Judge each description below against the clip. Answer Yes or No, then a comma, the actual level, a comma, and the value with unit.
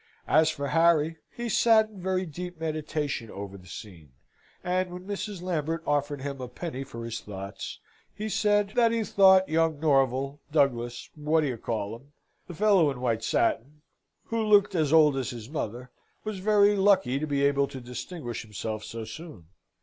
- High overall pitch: No, medium, 150 Hz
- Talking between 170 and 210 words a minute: Yes, average, 175 wpm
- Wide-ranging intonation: Yes, wide, 6.8 semitones